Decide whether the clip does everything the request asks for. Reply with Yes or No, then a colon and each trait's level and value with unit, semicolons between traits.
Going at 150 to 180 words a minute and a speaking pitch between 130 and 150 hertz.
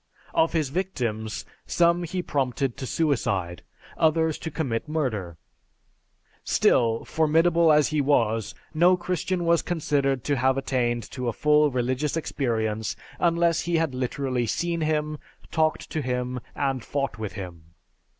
No: average, 140 wpm; medium, 140 Hz